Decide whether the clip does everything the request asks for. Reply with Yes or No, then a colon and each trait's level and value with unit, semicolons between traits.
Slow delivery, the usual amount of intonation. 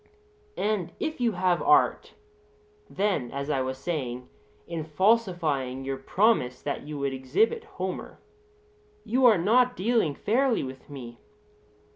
No: slow, 130 wpm; wide, 8.9 semitones